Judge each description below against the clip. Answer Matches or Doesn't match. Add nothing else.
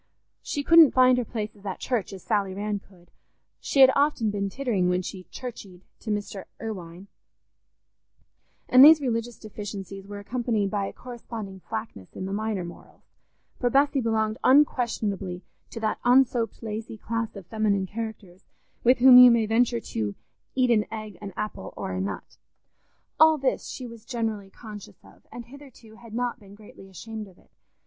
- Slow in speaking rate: Doesn't match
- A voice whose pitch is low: Doesn't match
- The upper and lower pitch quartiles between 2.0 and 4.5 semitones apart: Matches